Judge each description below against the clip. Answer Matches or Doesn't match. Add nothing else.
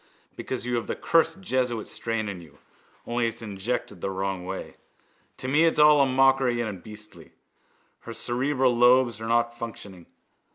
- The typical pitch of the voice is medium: Doesn't match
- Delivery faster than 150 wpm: Matches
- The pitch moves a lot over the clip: Doesn't match